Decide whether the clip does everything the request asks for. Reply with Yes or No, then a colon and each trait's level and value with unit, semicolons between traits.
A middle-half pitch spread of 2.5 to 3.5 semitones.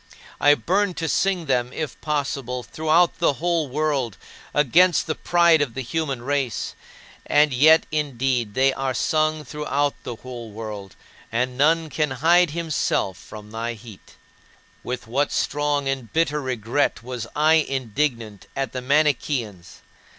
No: average, 4.1 semitones